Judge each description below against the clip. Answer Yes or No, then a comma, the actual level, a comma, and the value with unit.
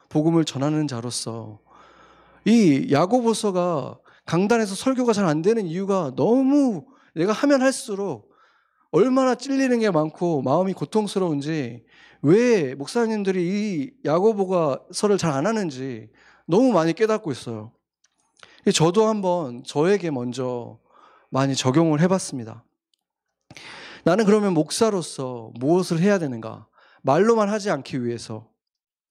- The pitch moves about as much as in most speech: No, wide, 8.1 semitones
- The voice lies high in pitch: No, medium, 175 Hz